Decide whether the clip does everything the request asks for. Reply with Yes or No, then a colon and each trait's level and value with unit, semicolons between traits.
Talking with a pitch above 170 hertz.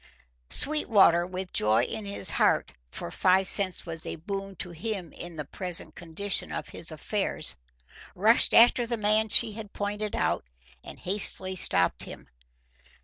Yes: high, 190 Hz